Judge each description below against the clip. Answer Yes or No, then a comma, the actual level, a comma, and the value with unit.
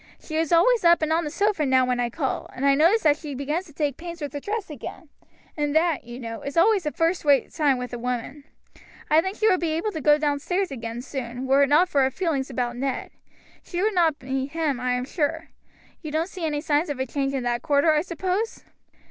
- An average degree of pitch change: Yes, average, 4.0 semitones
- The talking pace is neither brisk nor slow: No, fast, 245 wpm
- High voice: Yes, very high, 295 Hz